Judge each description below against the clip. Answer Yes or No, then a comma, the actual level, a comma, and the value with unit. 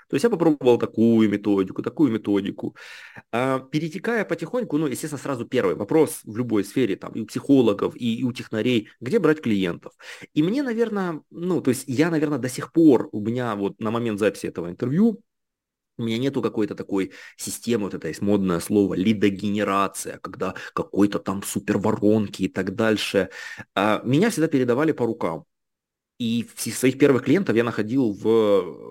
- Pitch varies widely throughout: Yes, wide, 5.9 semitones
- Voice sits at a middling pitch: No, low, 115 Hz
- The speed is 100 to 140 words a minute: No, fast, 160 wpm